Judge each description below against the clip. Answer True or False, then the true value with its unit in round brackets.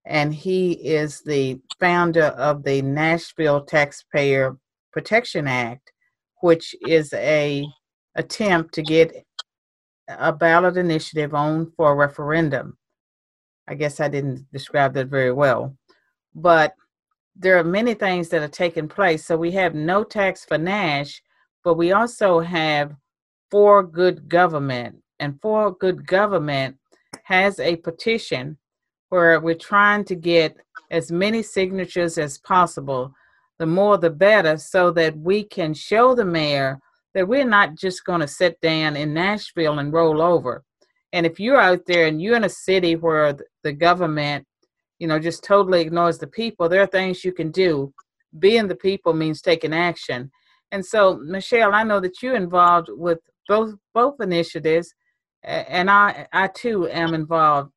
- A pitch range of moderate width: True (3.8 semitones)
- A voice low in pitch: False (170 Hz)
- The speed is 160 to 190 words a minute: False (150 wpm)